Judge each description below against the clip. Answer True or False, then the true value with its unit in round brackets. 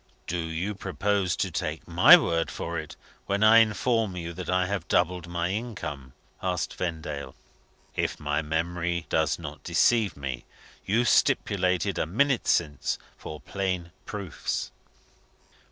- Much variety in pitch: False (3.7 semitones)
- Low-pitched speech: True (90 Hz)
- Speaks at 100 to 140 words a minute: True (135 wpm)